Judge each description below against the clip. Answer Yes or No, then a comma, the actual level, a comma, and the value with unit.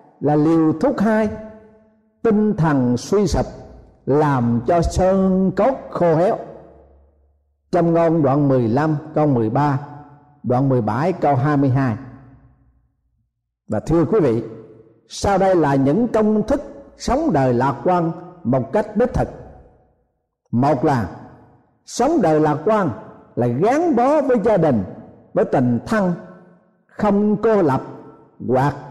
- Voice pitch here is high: No, medium, 155 Hz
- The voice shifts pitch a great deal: Yes, wide, 7.7 semitones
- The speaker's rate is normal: No, slow, 125 wpm